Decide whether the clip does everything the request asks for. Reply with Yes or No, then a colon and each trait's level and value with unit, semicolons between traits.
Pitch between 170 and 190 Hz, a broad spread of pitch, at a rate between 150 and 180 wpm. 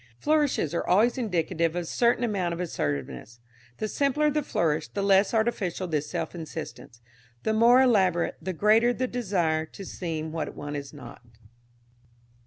Yes: medium, 185 Hz; wide, 6.7 semitones; average, 160 wpm